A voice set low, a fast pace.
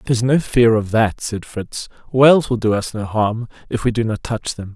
Yes: low, 115 Hz; fast, 250 wpm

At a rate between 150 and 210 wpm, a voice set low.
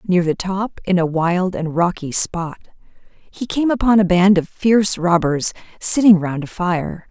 No: average, 175 wpm; medium, 185 Hz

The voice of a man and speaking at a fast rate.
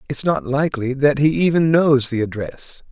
No: male; average, 185 wpm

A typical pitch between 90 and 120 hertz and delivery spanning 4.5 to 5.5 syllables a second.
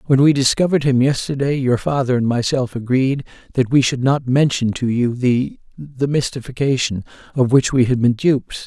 No: low, 130 Hz; 5.2 syllables/s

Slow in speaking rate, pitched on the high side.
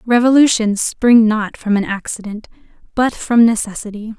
Yes: slow, 130 wpm; high, 225 Hz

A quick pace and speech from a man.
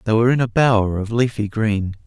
Yes: fast, 230 wpm; male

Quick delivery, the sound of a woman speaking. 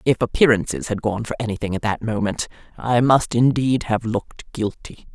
No: average, 175 wpm; female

